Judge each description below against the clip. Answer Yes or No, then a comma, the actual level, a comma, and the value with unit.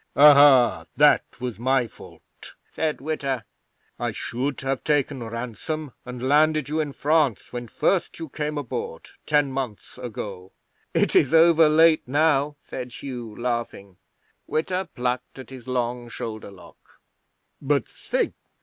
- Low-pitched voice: Yes, low, 130 Hz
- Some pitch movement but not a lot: Yes, average, 3.8 semitones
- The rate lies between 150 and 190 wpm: No, slow, 135 wpm